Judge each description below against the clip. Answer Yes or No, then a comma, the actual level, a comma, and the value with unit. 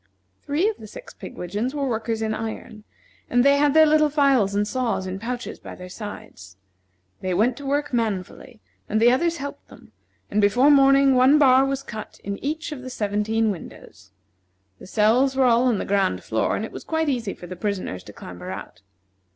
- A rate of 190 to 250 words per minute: Yes, average, 200 wpm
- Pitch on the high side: Yes, high, 235 Hz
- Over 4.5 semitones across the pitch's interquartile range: Yes, average, 5.2 semitones